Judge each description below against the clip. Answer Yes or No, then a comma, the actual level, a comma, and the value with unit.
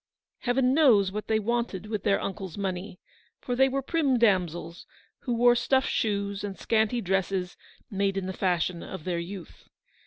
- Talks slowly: No, average, 165 wpm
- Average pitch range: Yes, average, 4.2 semitones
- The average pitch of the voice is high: Yes, high, 200 Hz